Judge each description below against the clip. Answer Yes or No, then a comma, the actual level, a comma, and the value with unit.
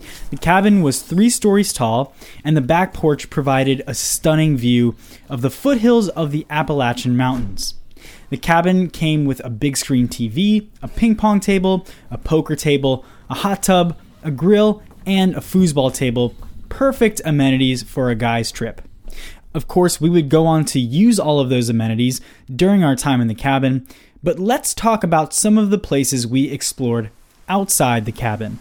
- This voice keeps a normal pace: Yes, average, 170 wpm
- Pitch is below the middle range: No, medium, 145 Hz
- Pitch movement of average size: No, wide, 6.8 semitones